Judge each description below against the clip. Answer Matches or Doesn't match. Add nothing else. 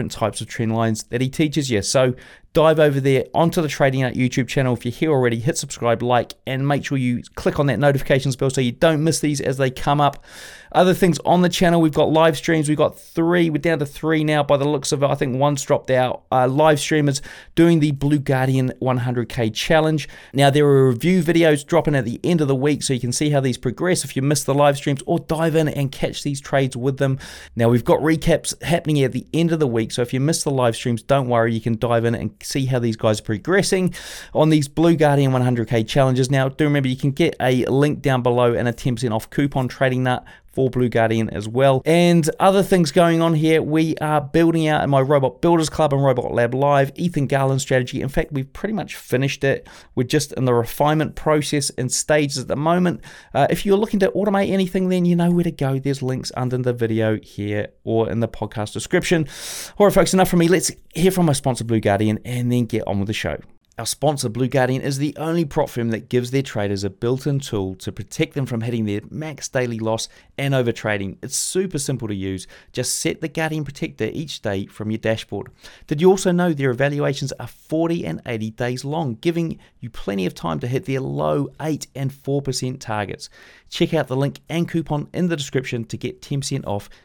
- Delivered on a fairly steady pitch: Doesn't match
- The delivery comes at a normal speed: Doesn't match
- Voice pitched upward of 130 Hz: Matches